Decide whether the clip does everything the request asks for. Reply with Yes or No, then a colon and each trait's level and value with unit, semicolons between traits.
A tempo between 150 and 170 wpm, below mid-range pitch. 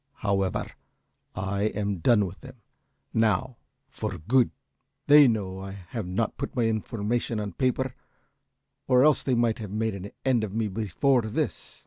Yes: average, 160 wpm; low, 110 Hz